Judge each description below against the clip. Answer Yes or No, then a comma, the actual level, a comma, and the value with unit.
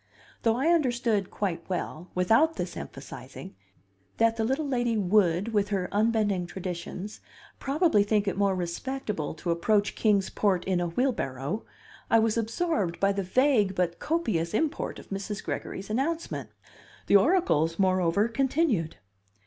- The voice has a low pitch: No, high, 205 Hz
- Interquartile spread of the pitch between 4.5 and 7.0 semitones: Yes, average, 4.9 semitones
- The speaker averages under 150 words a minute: Yes, average, 140 wpm